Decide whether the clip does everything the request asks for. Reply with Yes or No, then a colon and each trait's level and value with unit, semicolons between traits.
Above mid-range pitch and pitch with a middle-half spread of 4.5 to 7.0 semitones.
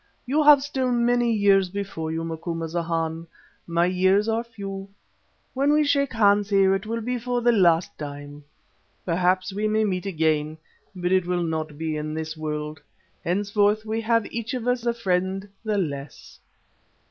Yes: high, 195 Hz; wide, 5.6 semitones